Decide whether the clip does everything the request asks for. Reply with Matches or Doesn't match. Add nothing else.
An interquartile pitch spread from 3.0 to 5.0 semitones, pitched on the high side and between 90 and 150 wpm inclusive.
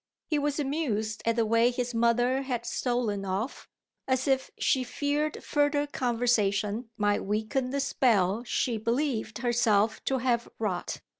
Matches